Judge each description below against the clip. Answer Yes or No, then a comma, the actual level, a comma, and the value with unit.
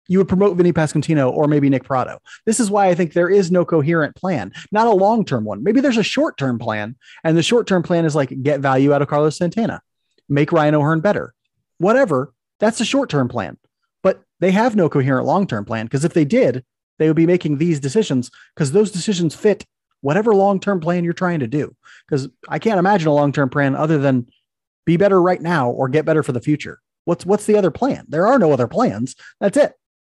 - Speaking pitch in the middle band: Yes, medium, 160 Hz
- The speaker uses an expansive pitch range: Yes, wide, 6.0 semitones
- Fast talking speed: Yes, fast, 220 wpm